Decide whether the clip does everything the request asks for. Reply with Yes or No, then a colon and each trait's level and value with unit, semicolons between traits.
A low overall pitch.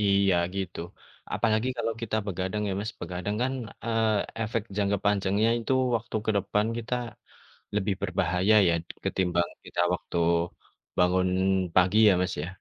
Yes: low, 100 Hz